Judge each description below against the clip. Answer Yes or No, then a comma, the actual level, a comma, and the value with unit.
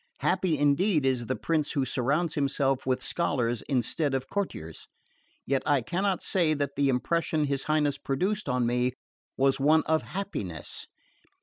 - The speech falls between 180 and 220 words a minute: No, average, 150 wpm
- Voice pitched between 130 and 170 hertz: Yes, medium, 140 Hz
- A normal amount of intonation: Yes, average, 3.4 semitones